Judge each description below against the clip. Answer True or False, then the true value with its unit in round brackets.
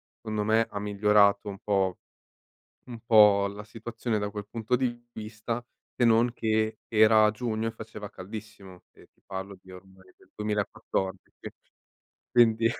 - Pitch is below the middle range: True (110 Hz)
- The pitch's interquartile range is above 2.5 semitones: False (2.0 semitones)